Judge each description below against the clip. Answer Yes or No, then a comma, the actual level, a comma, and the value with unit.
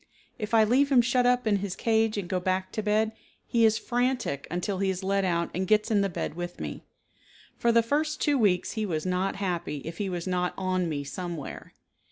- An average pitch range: Yes, average, 3.9 semitones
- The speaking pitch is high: Yes, high, 200 Hz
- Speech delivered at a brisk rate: Yes, fast, 225 wpm